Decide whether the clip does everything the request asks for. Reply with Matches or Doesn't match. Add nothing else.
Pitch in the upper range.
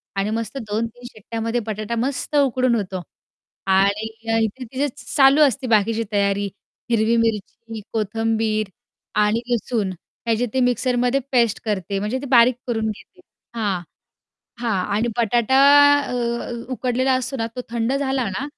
Matches